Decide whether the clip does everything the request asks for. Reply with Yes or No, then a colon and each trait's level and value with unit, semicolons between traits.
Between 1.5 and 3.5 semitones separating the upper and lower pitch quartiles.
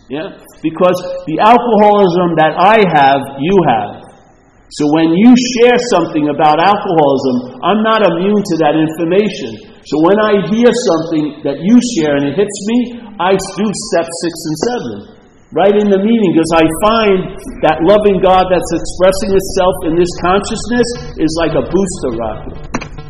No: average, 4.5 semitones